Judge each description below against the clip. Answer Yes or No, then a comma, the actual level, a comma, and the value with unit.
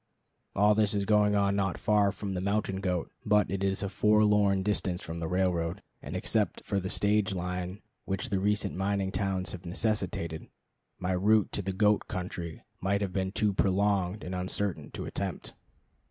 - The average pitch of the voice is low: Yes, very low, 95 Hz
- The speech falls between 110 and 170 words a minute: No, average, 180 wpm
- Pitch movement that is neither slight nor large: No, narrow, 2.0 semitones